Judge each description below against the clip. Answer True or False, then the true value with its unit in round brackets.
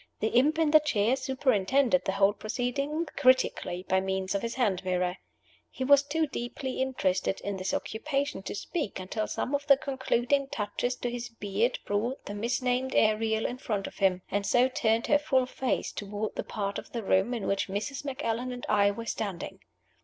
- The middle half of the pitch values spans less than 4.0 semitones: False (4.6 semitones)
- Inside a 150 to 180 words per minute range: False (190 wpm)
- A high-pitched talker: True (235 Hz)